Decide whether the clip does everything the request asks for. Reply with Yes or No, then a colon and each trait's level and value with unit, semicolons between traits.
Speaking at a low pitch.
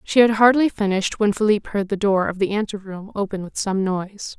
No: high, 205 Hz